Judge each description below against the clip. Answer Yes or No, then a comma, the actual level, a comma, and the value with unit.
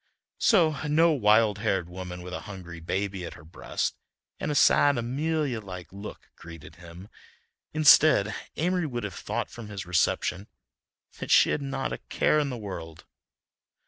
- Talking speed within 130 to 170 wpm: Yes, average, 160 wpm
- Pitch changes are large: Yes, wide, 7.9 semitones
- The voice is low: Yes, low, 105 Hz